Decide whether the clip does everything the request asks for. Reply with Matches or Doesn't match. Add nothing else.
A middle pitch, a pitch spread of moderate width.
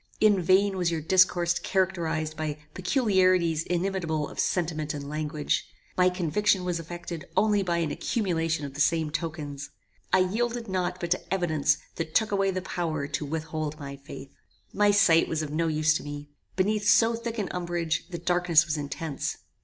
Matches